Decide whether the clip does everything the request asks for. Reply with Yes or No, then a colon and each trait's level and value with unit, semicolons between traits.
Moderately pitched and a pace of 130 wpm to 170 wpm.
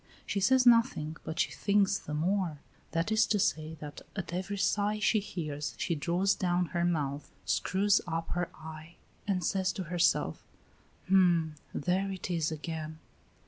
Yes: medium, 175 Hz; average, 160 wpm